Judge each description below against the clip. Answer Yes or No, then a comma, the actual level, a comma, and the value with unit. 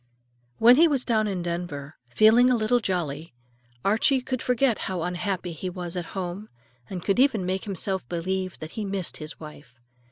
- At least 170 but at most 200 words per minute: Yes, average, 180 wpm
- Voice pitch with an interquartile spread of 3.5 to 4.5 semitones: Yes, average, 4.2 semitones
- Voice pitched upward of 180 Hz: Yes, high, 190 Hz